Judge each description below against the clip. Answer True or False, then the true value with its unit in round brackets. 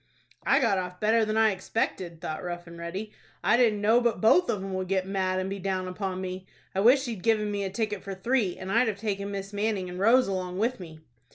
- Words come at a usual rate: False (245 wpm)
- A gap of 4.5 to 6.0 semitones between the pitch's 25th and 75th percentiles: False (2.9 semitones)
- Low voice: False (195 Hz)